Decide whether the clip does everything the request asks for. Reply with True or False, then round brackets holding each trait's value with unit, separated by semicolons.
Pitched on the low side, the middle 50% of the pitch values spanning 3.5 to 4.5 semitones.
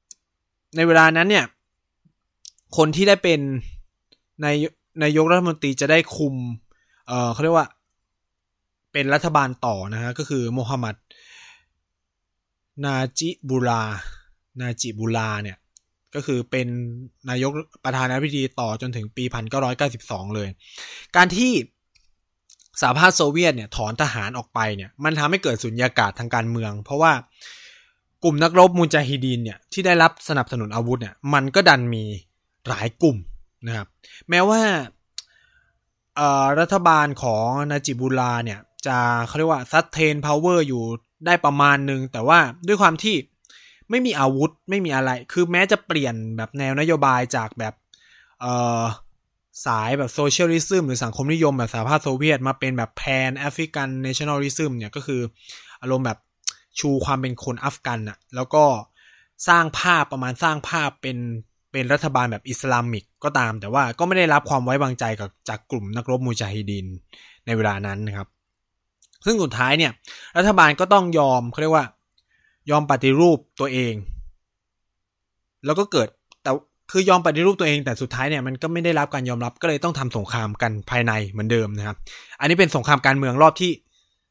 False (130 Hz; 5.4 semitones)